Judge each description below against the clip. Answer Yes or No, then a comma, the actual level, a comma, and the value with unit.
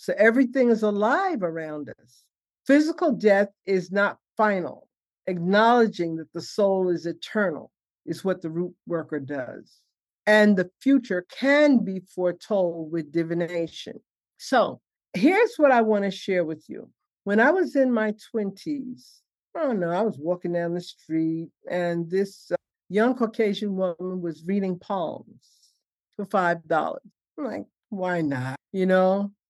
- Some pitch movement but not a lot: Yes, average, 4.3 semitones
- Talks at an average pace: Yes, average, 145 wpm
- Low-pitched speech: No, high, 190 Hz